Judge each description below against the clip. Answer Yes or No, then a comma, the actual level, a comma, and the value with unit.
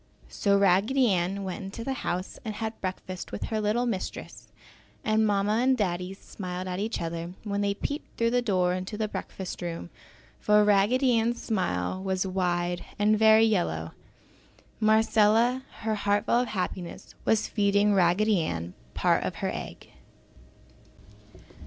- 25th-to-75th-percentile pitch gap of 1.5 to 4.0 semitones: Yes, average, 3.2 semitones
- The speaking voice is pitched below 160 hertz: No, high, 205 Hz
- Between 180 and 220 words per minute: No, average, 150 wpm